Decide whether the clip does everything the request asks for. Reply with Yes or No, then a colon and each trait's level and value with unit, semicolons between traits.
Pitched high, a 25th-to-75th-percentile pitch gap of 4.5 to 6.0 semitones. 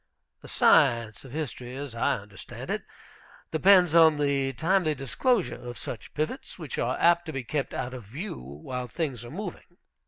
No: medium, 140 Hz; average, 5.2 semitones